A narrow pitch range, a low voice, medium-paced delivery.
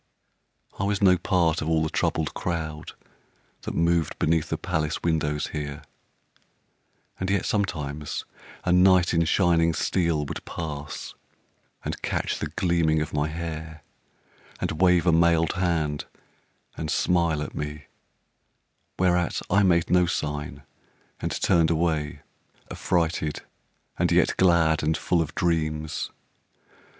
No: narrow, 2.2 semitones; very low, 80 Hz; slow, 130 wpm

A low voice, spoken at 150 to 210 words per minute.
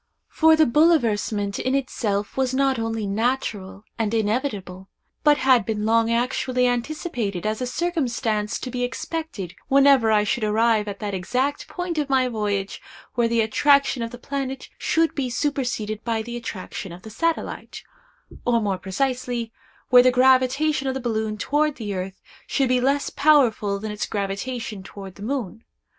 No: high, 240 Hz; average, 160 wpm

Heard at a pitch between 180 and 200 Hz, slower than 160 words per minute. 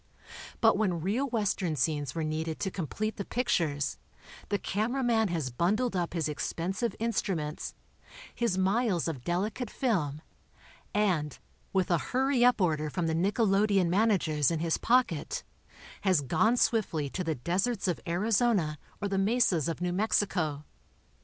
Yes: medium, 185 Hz; average, 150 wpm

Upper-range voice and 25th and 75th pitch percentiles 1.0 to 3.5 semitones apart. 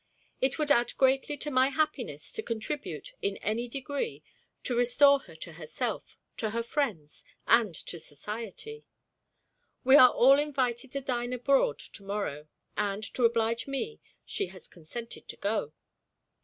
No: high, 240 Hz; average, 4.8 semitones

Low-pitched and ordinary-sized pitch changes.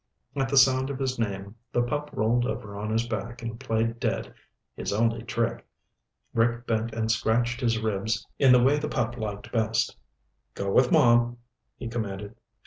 No: low, 115 Hz; narrow, 1.8 semitones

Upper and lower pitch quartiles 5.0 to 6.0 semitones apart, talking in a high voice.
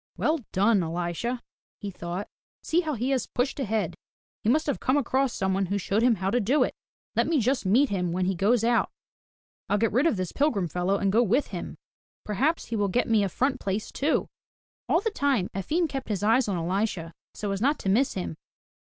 Yes: wide, 5.6 semitones; high, 215 Hz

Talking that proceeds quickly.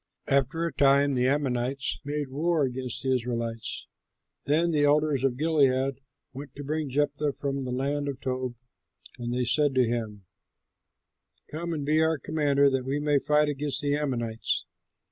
No: average, 165 wpm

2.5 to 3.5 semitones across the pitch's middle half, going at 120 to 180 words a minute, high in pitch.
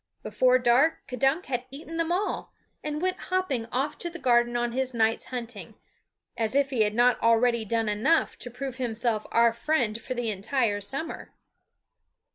Yes: average, 3.2 semitones; average, 170 wpm; high, 245 Hz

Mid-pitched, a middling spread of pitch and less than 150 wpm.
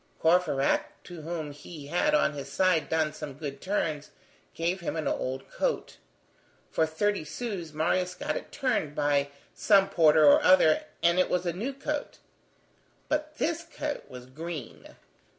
No: medium, 165 Hz; average, 4.4 semitones; average, 155 wpm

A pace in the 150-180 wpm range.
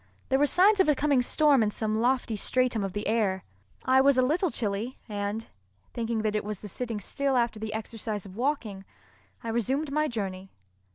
No: average, 195 wpm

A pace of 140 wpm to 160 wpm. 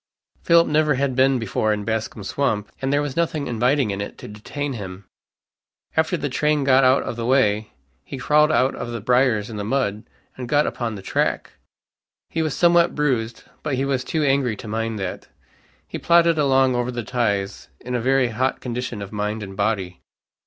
No: average, 195 wpm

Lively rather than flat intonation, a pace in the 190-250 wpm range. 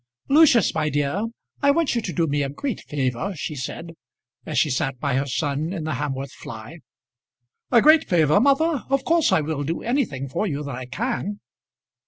Yes: wide, 9.0 semitones; average, 195 wpm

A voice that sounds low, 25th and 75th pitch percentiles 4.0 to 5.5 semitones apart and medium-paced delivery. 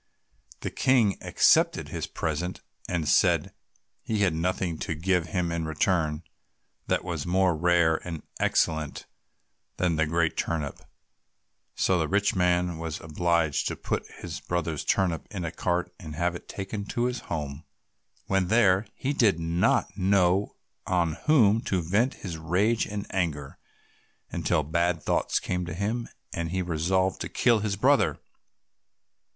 No: very low, 90 Hz; average, 3.0 semitones; average, 150 wpm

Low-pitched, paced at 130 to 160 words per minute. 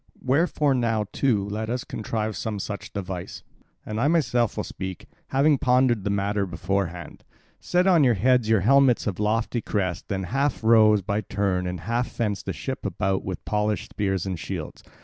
No: low, 105 Hz; average, 175 wpm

